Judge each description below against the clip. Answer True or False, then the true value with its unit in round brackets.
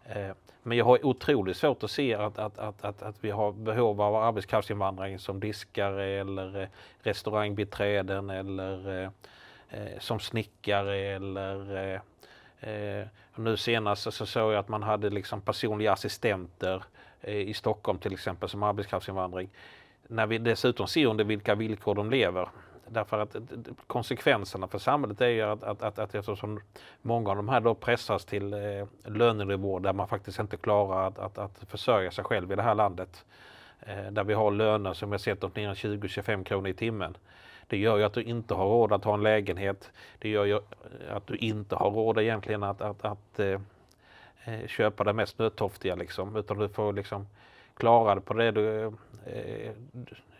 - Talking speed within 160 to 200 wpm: True (170 wpm)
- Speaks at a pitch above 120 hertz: False (105 Hz)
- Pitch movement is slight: True (1.8 semitones)